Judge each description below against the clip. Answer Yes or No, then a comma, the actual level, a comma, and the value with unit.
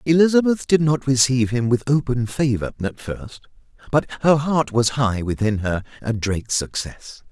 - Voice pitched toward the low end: Yes, low, 125 Hz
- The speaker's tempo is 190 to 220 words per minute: No, average, 165 wpm